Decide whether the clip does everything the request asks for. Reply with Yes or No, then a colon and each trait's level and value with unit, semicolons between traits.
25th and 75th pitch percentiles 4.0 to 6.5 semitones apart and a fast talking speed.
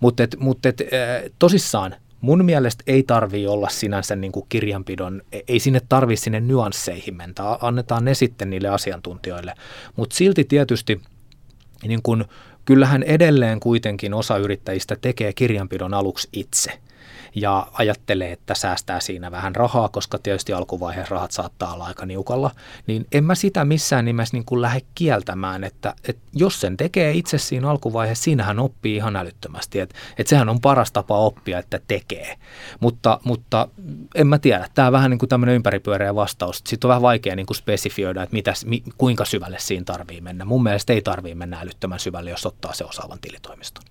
Yes: average, 4.4 semitones; fast, 165 wpm